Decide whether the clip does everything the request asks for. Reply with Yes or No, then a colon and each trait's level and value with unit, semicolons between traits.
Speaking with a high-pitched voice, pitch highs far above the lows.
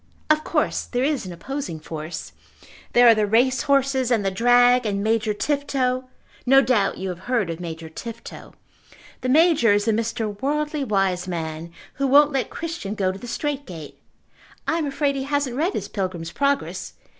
Yes: high, 240 Hz; wide, 6.1 semitones